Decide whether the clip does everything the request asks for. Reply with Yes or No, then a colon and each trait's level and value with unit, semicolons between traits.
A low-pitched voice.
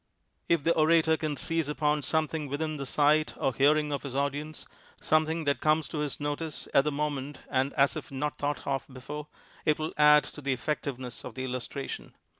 No: medium, 150 Hz